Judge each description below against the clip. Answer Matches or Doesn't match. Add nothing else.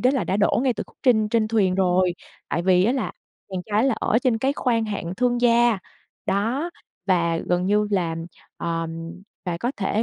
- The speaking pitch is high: Matches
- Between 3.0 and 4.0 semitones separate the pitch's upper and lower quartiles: Doesn't match